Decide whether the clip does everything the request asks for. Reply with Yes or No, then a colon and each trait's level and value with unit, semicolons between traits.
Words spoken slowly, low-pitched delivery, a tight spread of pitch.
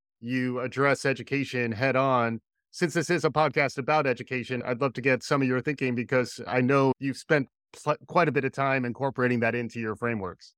No: fast, 205 wpm; low, 130 Hz; narrow, 2.2 semitones